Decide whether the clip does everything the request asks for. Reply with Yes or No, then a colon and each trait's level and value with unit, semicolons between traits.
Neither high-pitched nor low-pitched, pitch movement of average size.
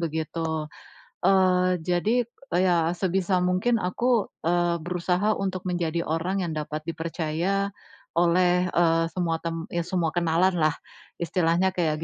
No: medium, 175 Hz; narrow, 1.9 semitones